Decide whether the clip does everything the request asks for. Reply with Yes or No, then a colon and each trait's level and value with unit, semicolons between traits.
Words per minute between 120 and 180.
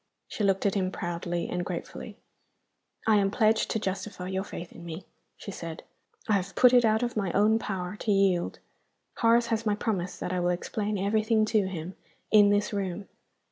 No: average, 190 wpm